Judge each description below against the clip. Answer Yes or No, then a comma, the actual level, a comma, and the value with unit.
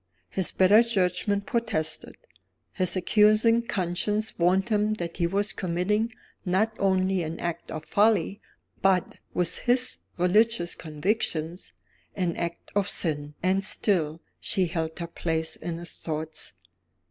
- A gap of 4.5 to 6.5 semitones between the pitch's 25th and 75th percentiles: No, average, 3.7 semitones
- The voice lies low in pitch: No, medium, 185 Hz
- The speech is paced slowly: Yes, slow, 130 wpm